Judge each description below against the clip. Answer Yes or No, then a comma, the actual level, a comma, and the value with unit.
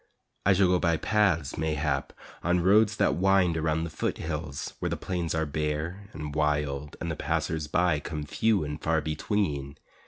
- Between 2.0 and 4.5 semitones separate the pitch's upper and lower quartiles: Yes, average, 3.1 semitones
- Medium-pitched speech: No, very low, 80 Hz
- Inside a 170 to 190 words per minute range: Yes, average, 175 wpm